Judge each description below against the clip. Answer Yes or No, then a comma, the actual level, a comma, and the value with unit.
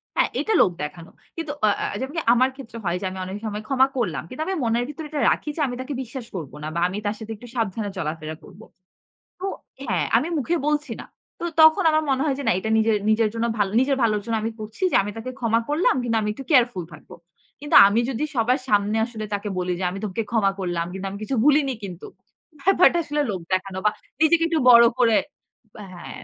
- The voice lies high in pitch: Yes, high, 230 Hz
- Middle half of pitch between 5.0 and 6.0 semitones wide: Yes, wide, 5.4 semitones